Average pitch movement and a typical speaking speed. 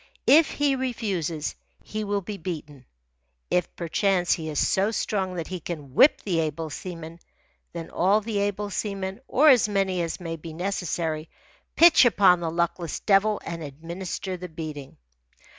Yes: average, 3.7 semitones; average, 160 wpm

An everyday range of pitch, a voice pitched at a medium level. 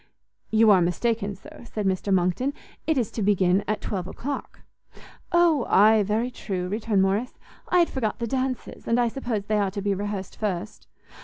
No: average, 3.5 semitones; high, 210 Hz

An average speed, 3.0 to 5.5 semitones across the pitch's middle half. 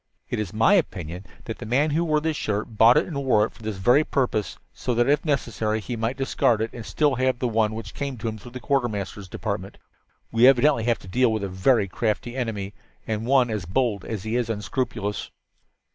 No: fast, 220 wpm; average, 3.6 semitones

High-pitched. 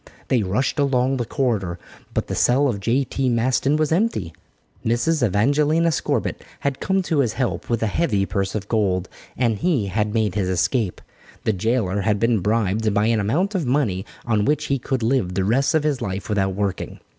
No: low, 115 Hz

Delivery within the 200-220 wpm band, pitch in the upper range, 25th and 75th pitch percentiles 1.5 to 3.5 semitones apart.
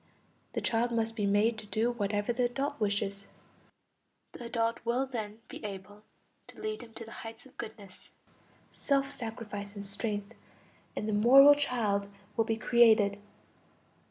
No: average, 155 wpm; high, 225 Hz; average, 2.7 semitones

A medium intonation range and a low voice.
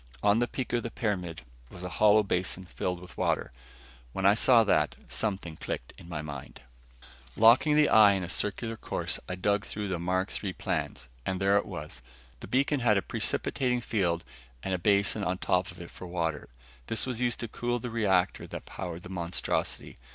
Yes: average, 3.9 semitones; very low, 95 Hz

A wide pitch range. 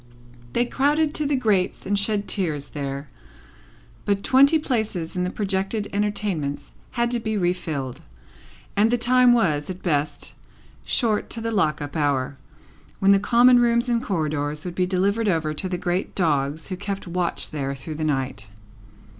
Yes: wide, 6.7 semitones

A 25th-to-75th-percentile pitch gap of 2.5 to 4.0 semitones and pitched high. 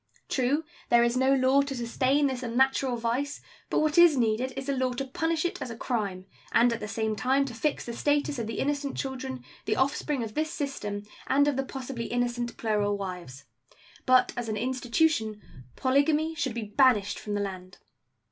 Yes: average, 3.5 semitones; very high, 255 Hz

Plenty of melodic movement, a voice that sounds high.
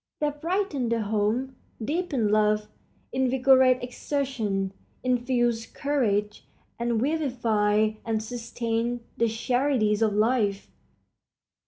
No: average, 3.4 semitones; high, 235 Hz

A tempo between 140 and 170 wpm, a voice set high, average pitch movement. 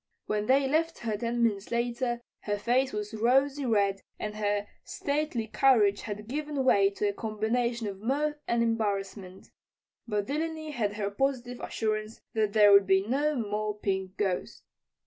Yes: average, 160 wpm; high, 220 Hz; average, 4.1 semitones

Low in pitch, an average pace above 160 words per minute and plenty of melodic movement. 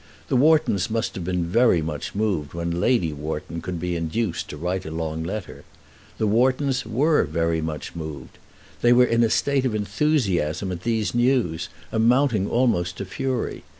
Yes: low, 100 Hz; average, 170 wpm; wide, 6.5 semitones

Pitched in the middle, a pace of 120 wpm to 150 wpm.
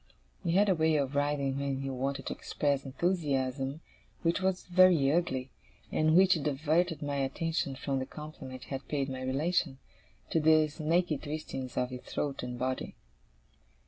No: medium, 145 Hz; average, 165 wpm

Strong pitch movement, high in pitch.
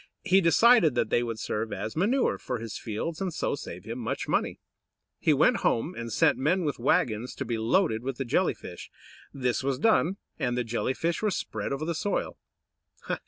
No: wide, 6.5 semitones; low, 130 Hz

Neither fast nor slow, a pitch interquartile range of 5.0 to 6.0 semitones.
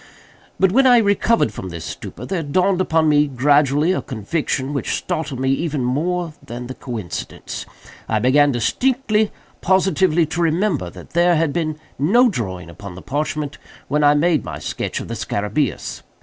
Yes: average, 170 wpm; wide, 5.6 semitones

